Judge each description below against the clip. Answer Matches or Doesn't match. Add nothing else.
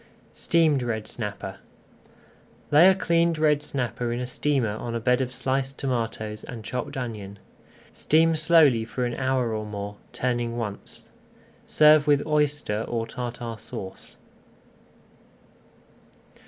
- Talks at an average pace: Doesn't match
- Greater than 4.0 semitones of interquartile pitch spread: Matches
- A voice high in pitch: Doesn't match